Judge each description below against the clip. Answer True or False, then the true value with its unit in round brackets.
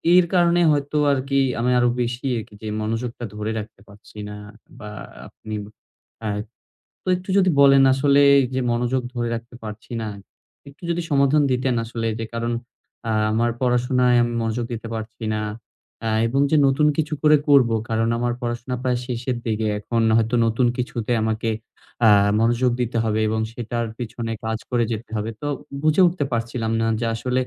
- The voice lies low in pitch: True (120 Hz)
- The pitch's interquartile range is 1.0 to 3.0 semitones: True (2.7 semitones)